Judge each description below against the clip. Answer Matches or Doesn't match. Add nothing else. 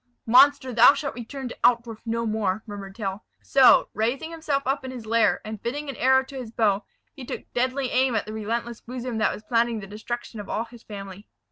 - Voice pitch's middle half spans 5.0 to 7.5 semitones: Doesn't match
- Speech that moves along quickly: Matches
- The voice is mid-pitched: Doesn't match